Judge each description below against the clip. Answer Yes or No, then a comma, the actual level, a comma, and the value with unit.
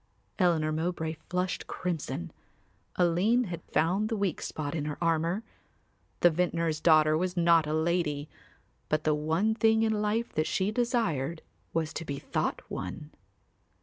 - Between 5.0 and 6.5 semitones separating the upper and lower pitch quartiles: No, average, 3.3 semitones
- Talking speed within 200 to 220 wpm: No, average, 150 wpm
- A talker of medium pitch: Yes, medium, 170 Hz